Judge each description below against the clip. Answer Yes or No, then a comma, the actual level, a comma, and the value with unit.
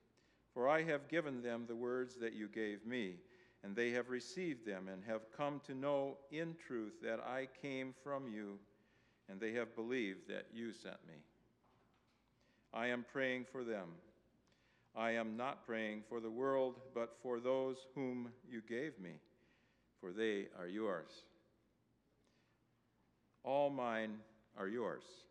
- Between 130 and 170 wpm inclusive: Yes, average, 150 wpm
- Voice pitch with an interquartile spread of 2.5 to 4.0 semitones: Yes, average, 3.0 semitones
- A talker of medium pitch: No, low, 120 Hz